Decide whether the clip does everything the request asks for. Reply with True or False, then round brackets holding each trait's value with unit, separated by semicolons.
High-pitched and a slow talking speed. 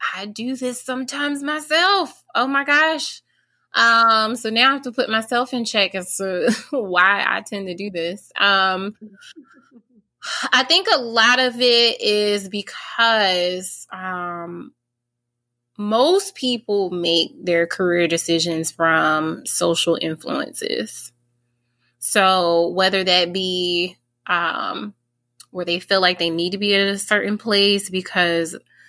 True (195 Hz; 130 wpm)